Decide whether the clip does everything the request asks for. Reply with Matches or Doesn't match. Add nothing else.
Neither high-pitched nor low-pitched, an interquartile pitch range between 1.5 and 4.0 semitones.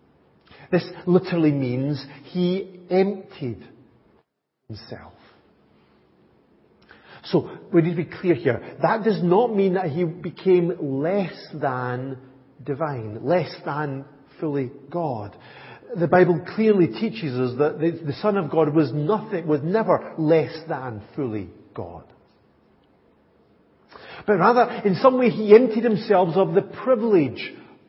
Doesn't match